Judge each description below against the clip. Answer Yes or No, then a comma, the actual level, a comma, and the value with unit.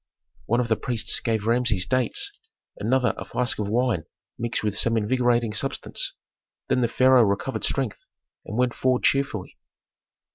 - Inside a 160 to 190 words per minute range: No, average, 150 wpm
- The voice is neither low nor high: No, low, 120 Hz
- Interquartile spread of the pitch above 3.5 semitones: No, average, 2.8 semitones